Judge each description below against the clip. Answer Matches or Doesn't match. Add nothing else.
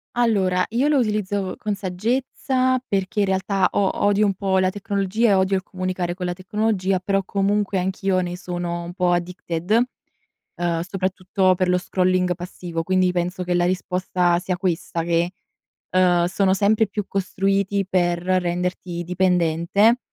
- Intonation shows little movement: Matches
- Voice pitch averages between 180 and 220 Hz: Matches